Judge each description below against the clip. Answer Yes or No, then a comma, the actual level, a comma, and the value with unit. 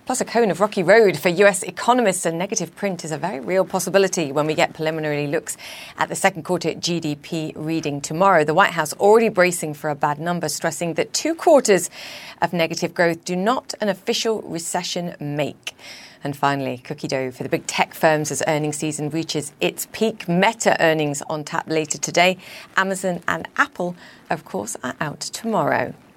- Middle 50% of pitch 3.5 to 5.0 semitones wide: Yes, average, 3.9 semitones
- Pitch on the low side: No, medium, 170 Hz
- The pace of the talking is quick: No, average, 180 wpm